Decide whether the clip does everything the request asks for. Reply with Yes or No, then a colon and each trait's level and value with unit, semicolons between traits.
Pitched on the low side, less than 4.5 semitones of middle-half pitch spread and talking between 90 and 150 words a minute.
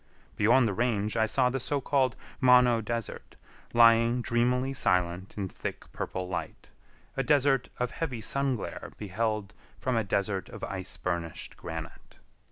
Yes: low, 115 Hz; average, 4.1 semitones; average, 145 wpm